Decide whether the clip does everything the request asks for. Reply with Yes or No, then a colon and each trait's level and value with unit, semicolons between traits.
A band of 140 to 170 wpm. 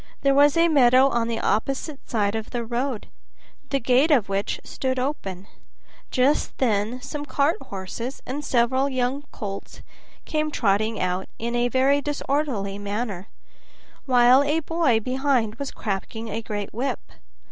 Yes: average, 145 wpm